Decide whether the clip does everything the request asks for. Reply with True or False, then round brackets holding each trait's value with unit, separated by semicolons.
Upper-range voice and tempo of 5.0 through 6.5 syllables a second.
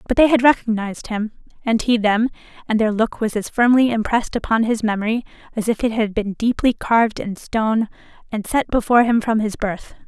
True (225 Hz; 5.7 syllables/s)